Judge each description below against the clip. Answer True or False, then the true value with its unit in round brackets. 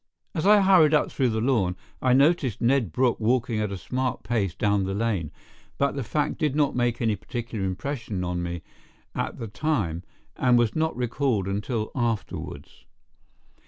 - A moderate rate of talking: True (170 wpm)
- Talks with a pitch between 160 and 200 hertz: False (120 Hz)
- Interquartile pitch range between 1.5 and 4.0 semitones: False (5.2 semitones)